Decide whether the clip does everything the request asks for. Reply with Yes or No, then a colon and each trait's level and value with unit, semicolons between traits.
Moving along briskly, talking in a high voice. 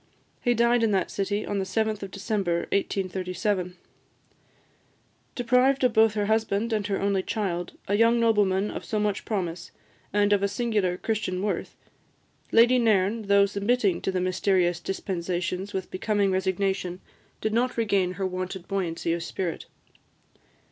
No: average, 150 wpm; high, 200 Hz